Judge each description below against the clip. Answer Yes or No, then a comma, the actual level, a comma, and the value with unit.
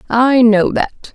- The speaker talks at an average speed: Yes, average, 155 wpm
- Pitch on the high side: Yes, high, 235 Hz